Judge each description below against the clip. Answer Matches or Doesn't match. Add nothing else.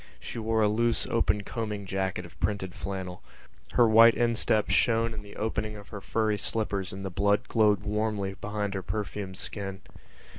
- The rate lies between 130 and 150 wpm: Doesn't match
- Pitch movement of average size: Doesn't match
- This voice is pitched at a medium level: Doesn't match